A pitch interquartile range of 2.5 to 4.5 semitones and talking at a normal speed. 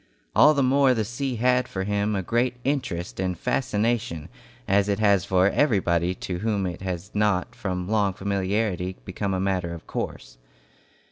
Yes: average, 3.6 semitones; average, 165 wpm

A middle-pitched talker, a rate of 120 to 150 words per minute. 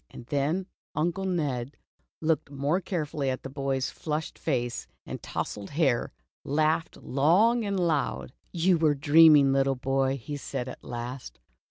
Yes: medium, 145 Hz; average, 145 wpm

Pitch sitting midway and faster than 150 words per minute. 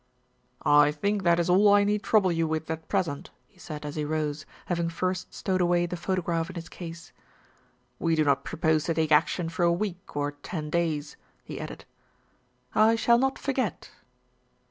Yes: medium, 170 Hz; average, 190 wpm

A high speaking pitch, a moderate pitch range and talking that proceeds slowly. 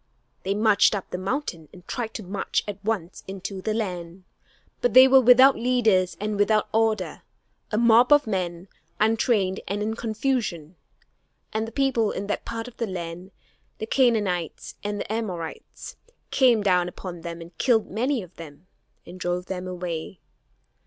No: high, 205 Hz; average, 4.0 semitones; average, 165 wpm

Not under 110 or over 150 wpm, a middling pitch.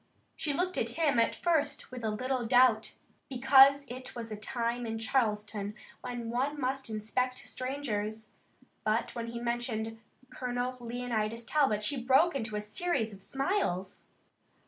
No: average, 145 wpm; high, 240 Hz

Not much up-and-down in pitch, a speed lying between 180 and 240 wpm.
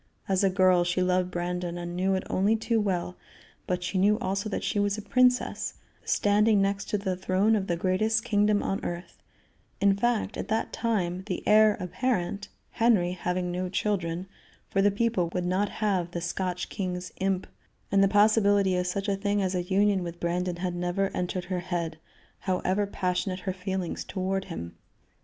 Yes: narrow, 2.2 semitones; average, 185 wpm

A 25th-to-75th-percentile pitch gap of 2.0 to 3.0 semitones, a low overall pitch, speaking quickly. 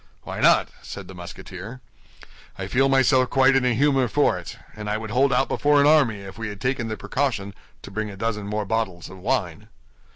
No: average, 5.0 semitones; low, 115 Hz; fast, 215 wpm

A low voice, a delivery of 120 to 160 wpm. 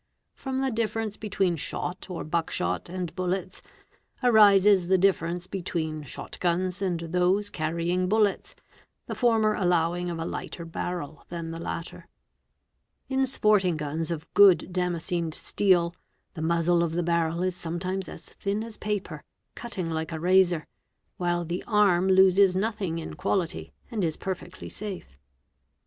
No: medium, 180 Hz; average, 150 wpm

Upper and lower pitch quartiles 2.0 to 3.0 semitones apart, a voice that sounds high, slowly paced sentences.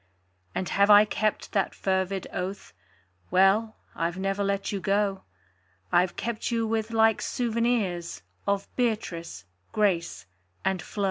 Yes: average, 2.7 semitones; high, 200 Hz; slow, 130 wpm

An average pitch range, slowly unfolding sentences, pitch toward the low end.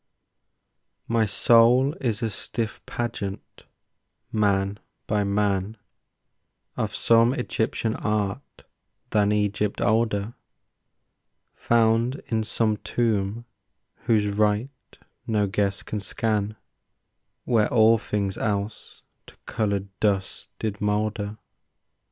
No: narrow, 2.0 semitones; slow, 95 wpm; low, 105 Hz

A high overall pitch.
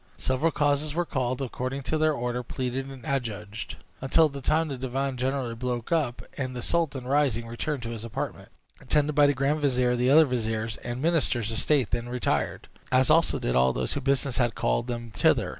No: low, 130 Hz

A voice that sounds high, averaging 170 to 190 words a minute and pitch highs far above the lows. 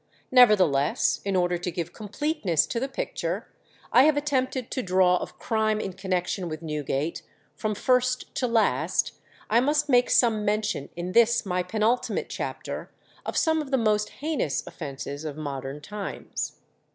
No: high, 210 Hz; average, 155 wpm; wide, 6.2 semitones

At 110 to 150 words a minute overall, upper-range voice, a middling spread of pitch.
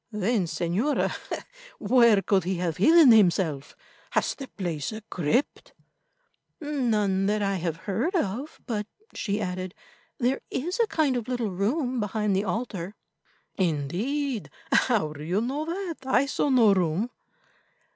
No: average, 140 wpm; high, 210 Hz; wide, 5.7 semitones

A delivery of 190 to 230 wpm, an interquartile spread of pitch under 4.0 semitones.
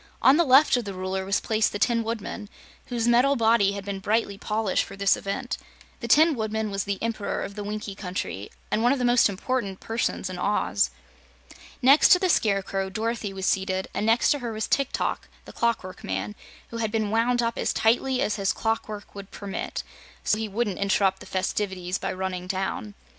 Yes: average, 200 wpm; average, 3.2 semitones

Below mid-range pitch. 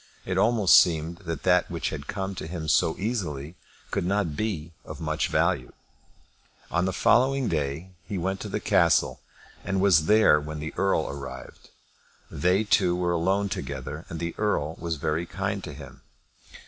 Yes: very low, 85 Hz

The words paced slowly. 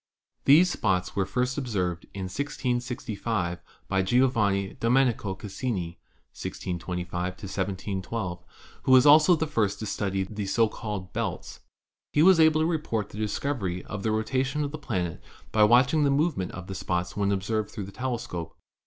No: average, 160 wpm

